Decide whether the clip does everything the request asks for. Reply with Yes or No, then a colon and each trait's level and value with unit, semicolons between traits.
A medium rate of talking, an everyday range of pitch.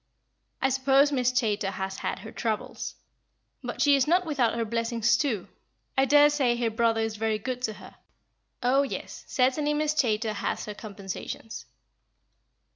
Yes: average, 155 wpm; average, 3.8 semitones